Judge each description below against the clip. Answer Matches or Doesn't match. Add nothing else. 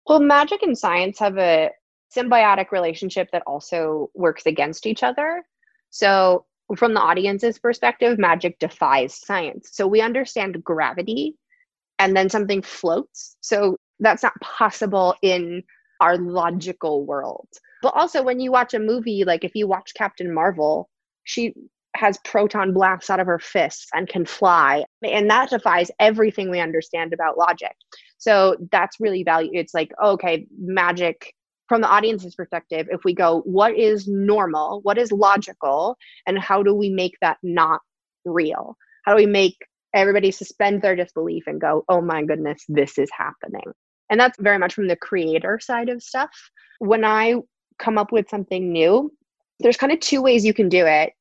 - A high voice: Matches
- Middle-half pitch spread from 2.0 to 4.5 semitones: Matches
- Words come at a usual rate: Matches